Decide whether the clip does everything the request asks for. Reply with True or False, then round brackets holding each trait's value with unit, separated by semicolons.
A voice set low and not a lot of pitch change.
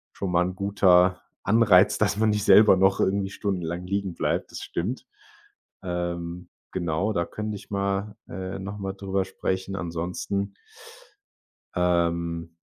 True (95 Hz; 2.2 semitones)